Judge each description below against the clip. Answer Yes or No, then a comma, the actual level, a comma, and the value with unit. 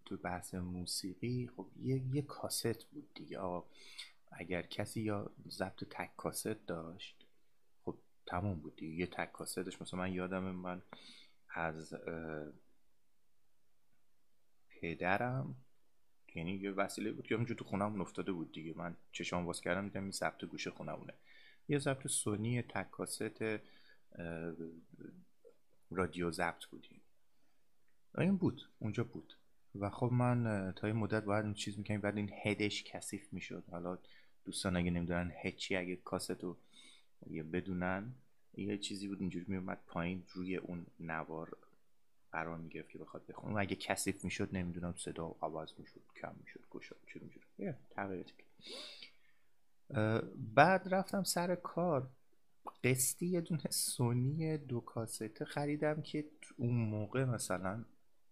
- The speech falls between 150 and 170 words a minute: No, average, 135 wpm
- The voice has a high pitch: No, low, 100 Hz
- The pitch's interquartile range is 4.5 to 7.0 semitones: Yes, wide, 5.5 semitones